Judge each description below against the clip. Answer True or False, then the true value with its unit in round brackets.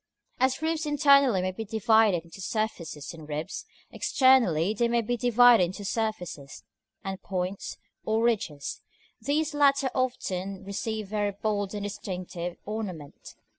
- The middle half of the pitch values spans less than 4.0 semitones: False (4.7 semitones)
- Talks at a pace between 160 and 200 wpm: False (140 wpm)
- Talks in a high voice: True (210 Hz)